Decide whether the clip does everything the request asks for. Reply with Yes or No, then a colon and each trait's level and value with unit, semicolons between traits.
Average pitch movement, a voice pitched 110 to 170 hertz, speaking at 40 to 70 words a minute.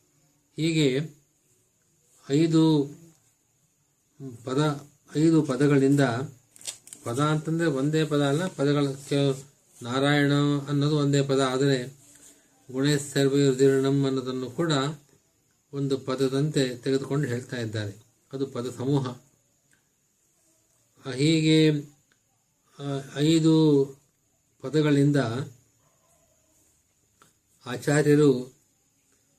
No: narrow, 1.7 semitones; medium, 140 Hz; slow, 65 wpm